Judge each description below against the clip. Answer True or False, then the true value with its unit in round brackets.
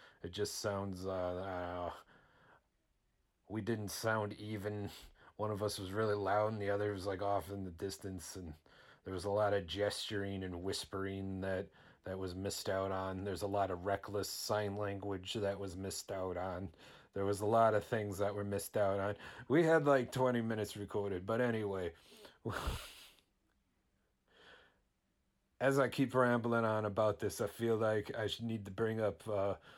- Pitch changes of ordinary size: False (2.1 semitones)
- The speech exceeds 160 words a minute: True (175 wpm)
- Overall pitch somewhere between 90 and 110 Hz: True (100 Hz)